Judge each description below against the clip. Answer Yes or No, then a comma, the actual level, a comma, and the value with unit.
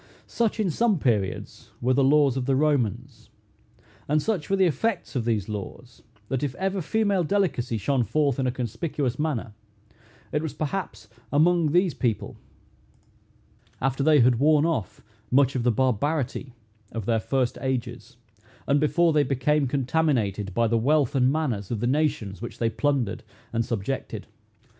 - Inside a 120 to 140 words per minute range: No, average, 160 wpm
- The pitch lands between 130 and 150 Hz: Yes, low, 135 Hz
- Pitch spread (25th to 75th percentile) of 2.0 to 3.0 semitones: No, average, 4.5 semitones